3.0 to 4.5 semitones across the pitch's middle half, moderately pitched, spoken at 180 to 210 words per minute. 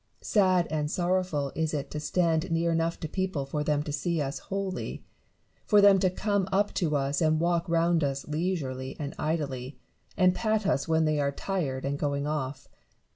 Yes: average, 4.1 semitones; medium, 160 Hz; average, 185 wpm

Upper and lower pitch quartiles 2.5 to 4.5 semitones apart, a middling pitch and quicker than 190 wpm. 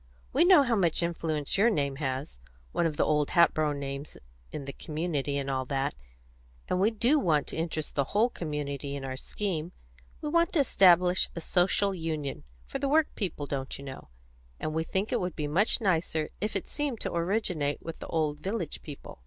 No: wide, 5.4 semitones; medium, 160 Hz; average, 200 wpm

